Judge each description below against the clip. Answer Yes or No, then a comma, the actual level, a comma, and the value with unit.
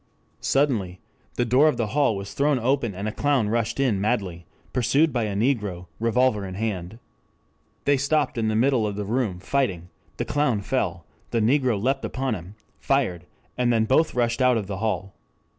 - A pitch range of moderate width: Yes, average, 4.7 semitones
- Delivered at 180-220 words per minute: Yes, average, 185 wpm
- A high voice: No, low, 115 Hz